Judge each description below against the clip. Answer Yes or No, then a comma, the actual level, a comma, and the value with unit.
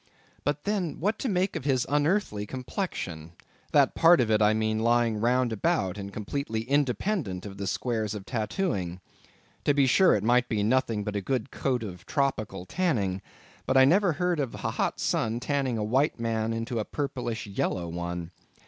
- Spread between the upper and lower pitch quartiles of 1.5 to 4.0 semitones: No, average, 5.3 semitones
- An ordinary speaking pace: Yes, average, 185 wpm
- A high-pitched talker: No, low, 115 Hz